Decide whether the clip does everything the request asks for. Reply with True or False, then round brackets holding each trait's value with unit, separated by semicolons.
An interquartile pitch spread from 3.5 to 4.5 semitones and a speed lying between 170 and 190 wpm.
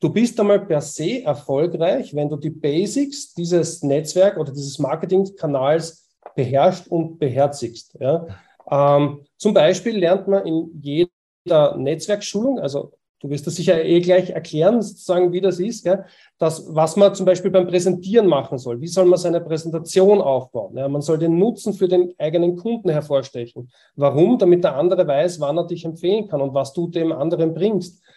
True (4.2 semitones; 175 wpm)